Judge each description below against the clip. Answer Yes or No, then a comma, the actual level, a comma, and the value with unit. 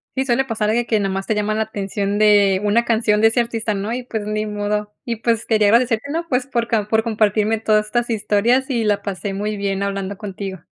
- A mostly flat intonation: Yes, narrow, 2.1 semitones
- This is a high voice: Yes, high, 215 Hz